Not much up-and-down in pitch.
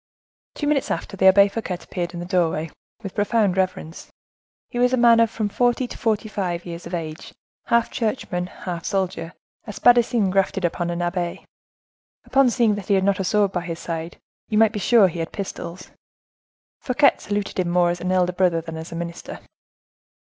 No: average, 3.8 semitones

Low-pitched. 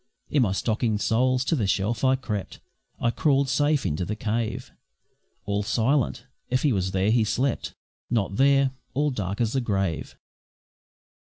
Yes: low, 115 Hz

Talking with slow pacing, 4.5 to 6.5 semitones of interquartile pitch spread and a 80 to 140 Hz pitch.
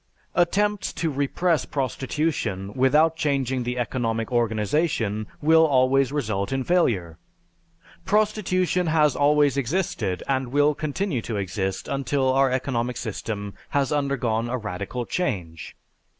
Yes: slow, 120 wpm; average, 5.1 semitones; low, 135 Hz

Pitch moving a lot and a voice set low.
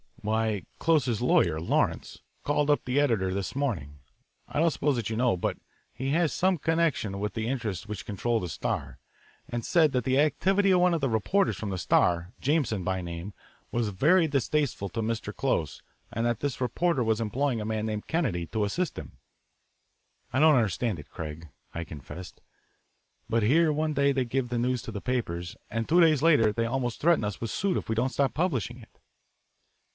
Yes: wide, 5.8 semitones; low, 120 Hz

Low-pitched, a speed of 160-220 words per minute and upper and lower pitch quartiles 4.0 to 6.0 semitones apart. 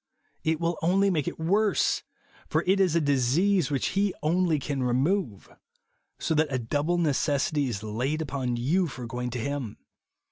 No: medium, 150 Hz; average, 170 wpm; average, 5.3 semitones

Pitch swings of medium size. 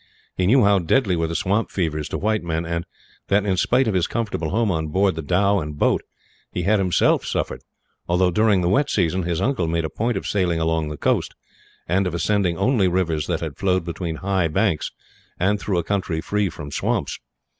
Yes: average, 3.6 semitones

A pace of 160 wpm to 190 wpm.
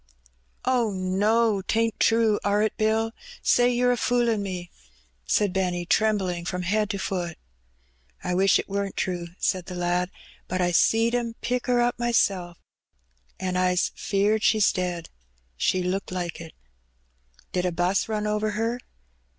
Yes: average, 165 wpm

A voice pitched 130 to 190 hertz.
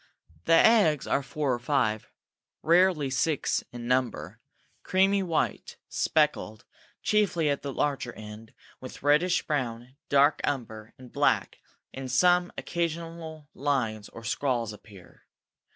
Yes: medium, 140 Hz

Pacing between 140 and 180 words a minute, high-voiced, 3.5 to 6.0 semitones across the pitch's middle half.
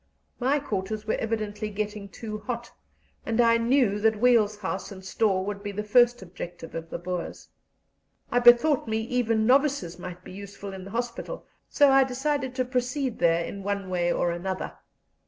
Yes: average, 175 wpm; high, 215 Hz; average, 4.2 semitones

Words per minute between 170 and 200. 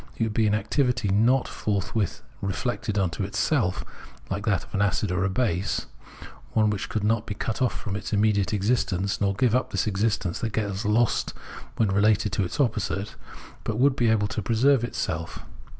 Yes: average, 195 wpm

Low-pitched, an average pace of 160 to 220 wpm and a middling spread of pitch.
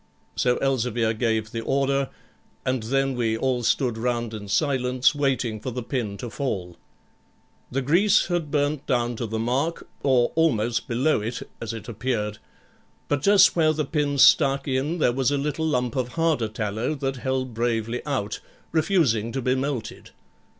Yes: low, 130 Hz; average, 165 wpm; average, 3.6 semitones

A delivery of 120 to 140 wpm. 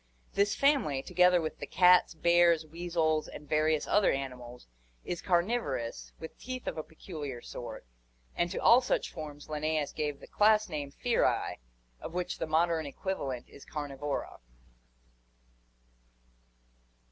Yes: slow, 135 wpm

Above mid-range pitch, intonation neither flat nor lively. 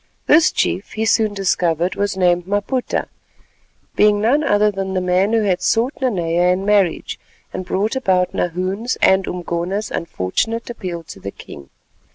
Yes: high, 195 Hz; average, 3.2 semitones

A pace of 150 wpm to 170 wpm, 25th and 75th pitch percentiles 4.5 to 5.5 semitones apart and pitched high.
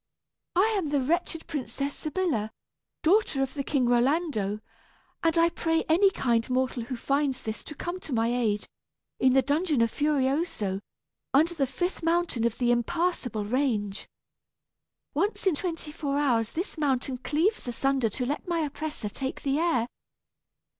Yes: average, 155 wpm; average, 5.1 semitones; very high, 280 Hz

